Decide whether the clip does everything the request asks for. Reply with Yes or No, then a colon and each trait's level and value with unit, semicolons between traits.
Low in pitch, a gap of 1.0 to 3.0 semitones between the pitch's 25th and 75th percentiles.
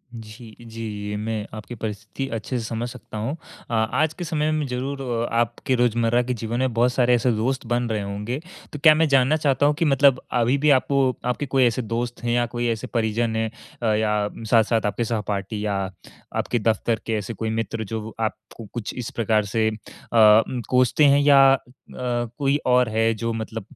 Yes: low, 115 Hz; narrow, 2.5 semitones